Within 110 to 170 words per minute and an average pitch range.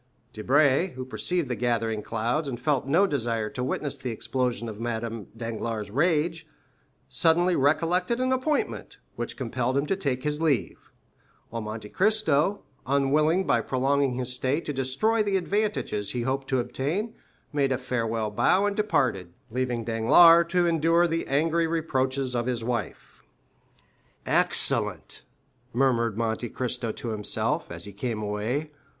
No: average, 150 wpm; wide, 5.9 semitones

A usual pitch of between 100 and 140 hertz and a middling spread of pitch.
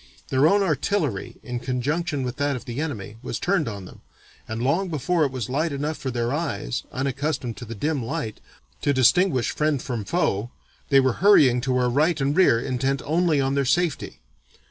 Yes: low, 135 Hz; average, 4.1 semitones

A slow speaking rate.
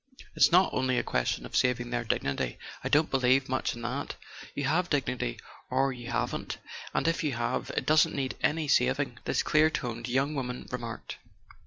No: average, 185 wpm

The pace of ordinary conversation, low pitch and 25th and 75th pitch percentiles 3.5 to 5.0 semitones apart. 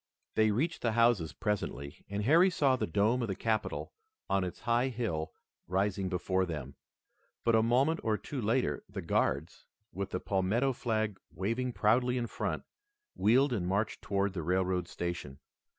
Yes: average, 165 wpm; low, 105 Hz; average, 4.4 semitones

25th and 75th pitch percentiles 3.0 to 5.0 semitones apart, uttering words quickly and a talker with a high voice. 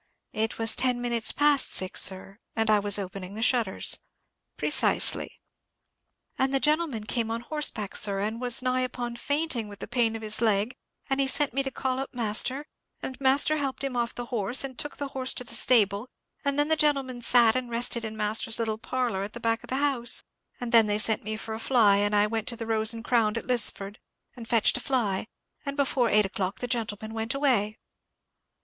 Yes: average, 3.3 semitones; fast, 210 wpm; high, 235 Hz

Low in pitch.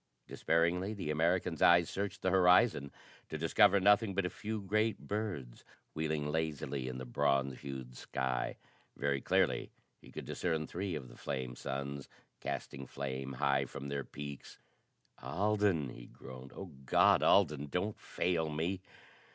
Yes: very low, 80 Hz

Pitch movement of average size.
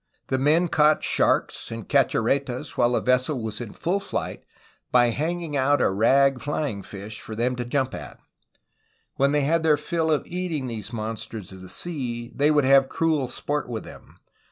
Yes: average, 4.2 semitones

